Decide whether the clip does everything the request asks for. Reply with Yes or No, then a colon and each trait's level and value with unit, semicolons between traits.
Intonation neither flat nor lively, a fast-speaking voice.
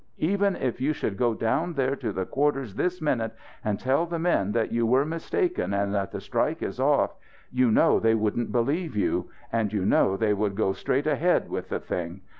No: wide, 6.2 semitones; fast, 210 wpm